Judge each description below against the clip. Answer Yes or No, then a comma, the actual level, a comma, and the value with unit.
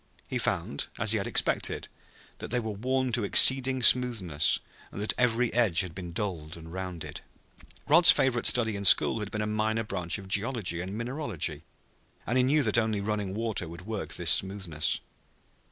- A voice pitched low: Yes, low, 105 Hz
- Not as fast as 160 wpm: No, average, 180 wpm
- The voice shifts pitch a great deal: No, average, 4.7 semitones